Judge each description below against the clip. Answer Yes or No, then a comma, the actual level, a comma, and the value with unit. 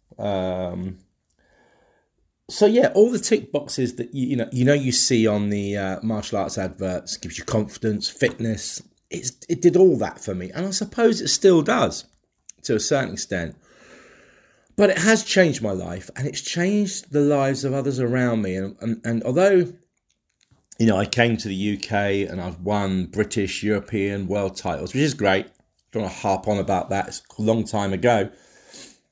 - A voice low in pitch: Yes, low, 110 Hz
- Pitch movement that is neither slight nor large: No, wide, 6.7 semitones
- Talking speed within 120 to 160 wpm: No, average, 190 wpm